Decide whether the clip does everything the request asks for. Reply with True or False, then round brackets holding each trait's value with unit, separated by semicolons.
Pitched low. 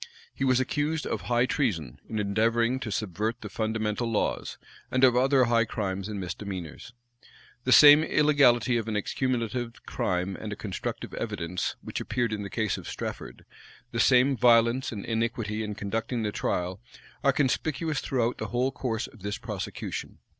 True (115 Hz)